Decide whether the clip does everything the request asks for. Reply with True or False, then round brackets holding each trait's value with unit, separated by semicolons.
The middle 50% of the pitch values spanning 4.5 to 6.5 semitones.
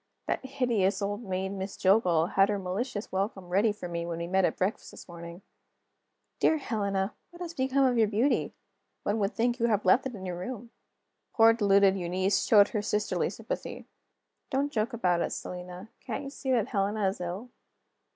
False (3.9 semitones)